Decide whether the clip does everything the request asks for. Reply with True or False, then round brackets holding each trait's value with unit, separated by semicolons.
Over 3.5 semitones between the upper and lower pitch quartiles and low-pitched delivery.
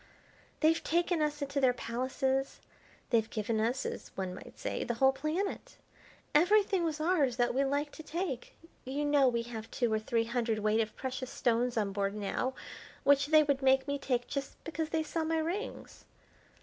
False (4.6 semitones; 270 Hz)